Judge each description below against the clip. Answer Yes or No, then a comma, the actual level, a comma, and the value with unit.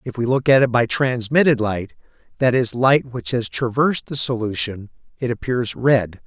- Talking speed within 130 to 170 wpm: No, average, 180 wpm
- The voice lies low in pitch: Yes, low, 125 Hz